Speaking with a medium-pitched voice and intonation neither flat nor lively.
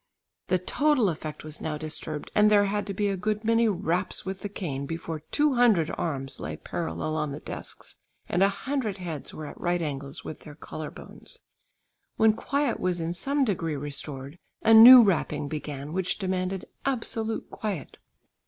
No: medium, 180 Hz; wide, 5.7 semitones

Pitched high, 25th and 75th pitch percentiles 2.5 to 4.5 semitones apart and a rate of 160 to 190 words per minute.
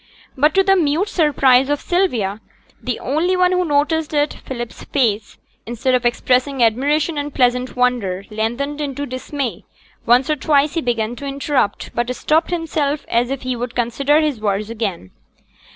Yes: very high, 270 Hz; average, 3.9 semitones; average, 165 wpm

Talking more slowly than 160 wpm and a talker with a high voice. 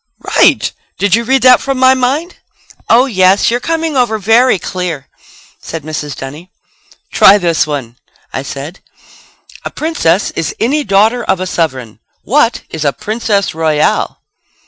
Yes: average, 145 wpm; high, 200 Hz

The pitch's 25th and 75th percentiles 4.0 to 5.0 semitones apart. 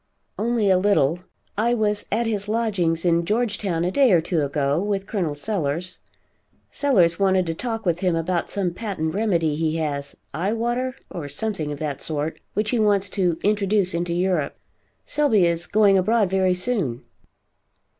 Yes: average, 4.4 semitones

